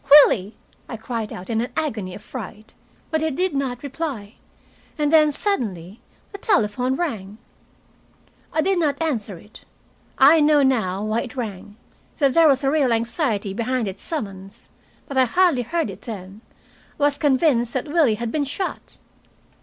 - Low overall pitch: No, very high, 255 Hz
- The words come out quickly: No, average, 160 wpm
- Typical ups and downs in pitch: No, wide, 5.8 semitones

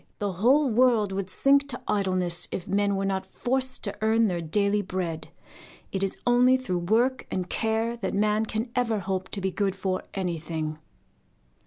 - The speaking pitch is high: Yes, high, 200 Hz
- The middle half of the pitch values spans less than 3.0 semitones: No, average, 3.7 semitones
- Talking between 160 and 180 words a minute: Yes, average, 175 wpm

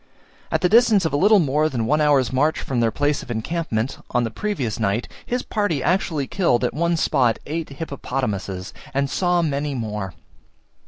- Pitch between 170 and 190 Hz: No, medium, 140 Hz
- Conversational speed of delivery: Yes, average, 180 wpm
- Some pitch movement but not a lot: No, wide, 5.8 semitones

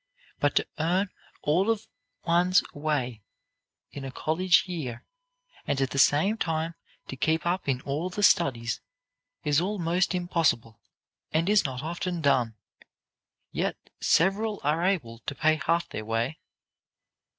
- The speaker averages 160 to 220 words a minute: No, average, 140 wpm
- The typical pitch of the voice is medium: Yes, medium, 160 Hz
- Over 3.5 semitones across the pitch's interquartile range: Yes, average, 4.8 semitones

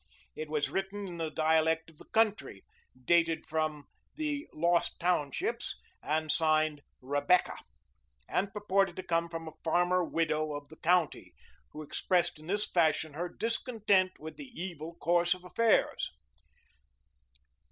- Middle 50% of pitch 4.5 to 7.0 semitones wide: No, average, 2.9 semitones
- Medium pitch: Yes, medium, 170 Hz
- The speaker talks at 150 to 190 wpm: No, average, 140 wpm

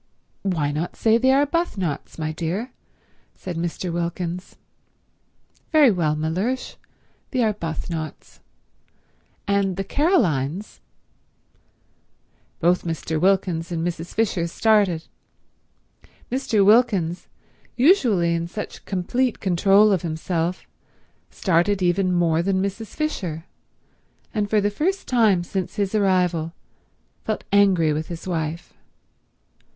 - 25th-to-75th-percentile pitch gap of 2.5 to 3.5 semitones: No, average, 4.1 semitones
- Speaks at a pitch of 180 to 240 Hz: Yes, medium, 185 Hz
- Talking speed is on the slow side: Yes, slow, 105 wpm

